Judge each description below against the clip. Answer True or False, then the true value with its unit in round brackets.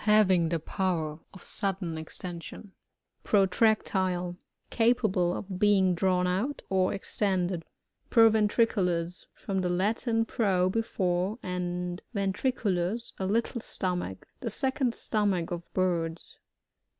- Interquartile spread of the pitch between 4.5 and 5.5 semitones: False (3.1 semitones)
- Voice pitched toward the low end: False (190 Hz)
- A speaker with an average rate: False (115 wpm)